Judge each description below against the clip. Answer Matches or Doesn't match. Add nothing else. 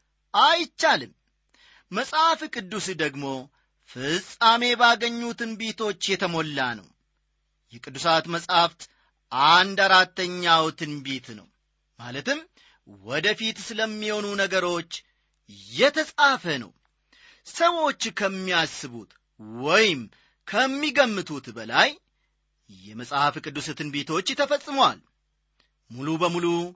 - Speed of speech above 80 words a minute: Doesn't match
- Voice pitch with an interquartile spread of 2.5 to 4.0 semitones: Doesn't match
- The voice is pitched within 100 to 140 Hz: Doesn't match